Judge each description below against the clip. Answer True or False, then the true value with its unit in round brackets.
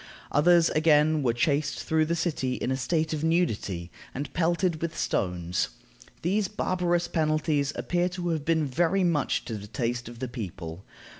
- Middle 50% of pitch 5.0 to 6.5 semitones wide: True (5.6 semitones)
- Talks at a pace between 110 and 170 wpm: True (165 wpm)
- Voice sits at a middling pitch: True (155 Hz)